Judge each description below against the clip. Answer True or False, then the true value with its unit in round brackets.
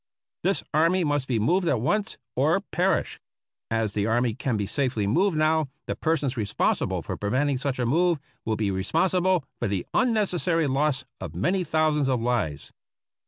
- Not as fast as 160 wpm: False (170 wpm)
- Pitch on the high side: False (140 Hz)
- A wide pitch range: True (6.7 semitones)